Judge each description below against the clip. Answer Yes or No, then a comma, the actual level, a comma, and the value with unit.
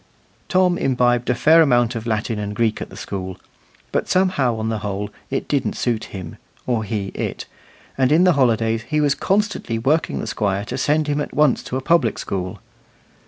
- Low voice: Yes, low, 120 Hz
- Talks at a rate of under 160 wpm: No, average, 195 wpm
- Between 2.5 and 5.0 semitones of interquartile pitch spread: No, wide, 5.4 semitones